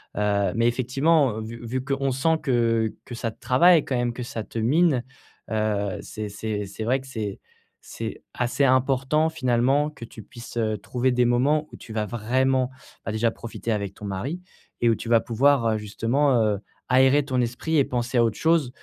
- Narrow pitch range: No, average, 3.3 semitones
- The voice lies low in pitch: Yes, low, 120 Hz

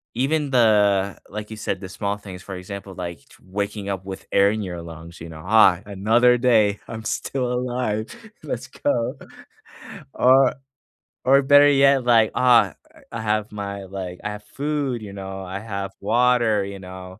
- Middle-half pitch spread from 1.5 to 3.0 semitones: No, average, 4.0 semitones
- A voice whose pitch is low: Yes, low, 105 Hz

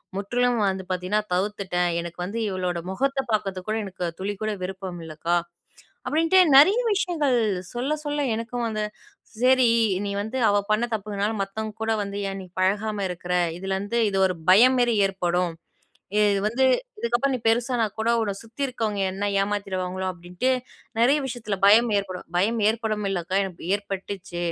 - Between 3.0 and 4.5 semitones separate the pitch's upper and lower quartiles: Yes, average, 3.9 semitones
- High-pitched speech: Yes, high, 205 Hz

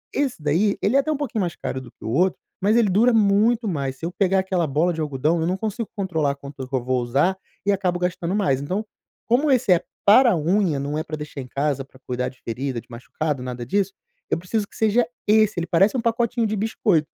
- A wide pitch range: Yes, wide, 6.9 semitones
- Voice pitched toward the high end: No, medium, 180 Hz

